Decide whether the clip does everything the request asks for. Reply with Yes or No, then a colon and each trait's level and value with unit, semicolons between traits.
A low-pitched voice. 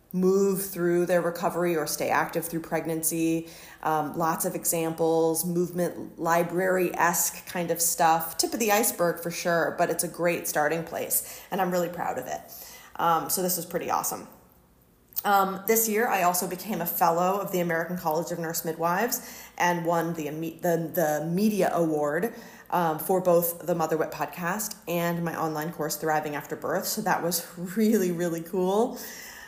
No: medium, 170 Hz